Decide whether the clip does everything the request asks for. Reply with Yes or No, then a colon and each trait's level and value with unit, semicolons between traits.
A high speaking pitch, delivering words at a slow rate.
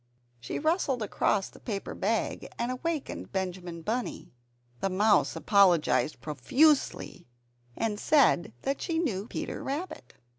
Yes: high, 215 Hz; slow, 120 wpm